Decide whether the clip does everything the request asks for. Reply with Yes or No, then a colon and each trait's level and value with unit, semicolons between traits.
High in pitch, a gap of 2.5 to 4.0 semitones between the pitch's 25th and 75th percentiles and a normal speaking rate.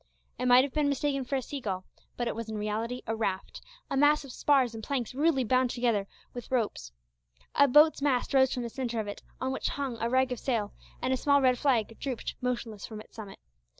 No: very high, 250 Hz; average, 3.3 semitones; fast, 225 wpm